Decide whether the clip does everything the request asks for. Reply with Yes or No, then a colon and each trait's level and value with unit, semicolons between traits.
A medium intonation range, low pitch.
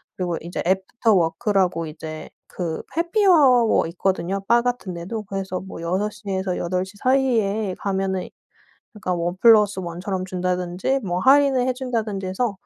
No: average, 4.2 semitones; high, 195 Hz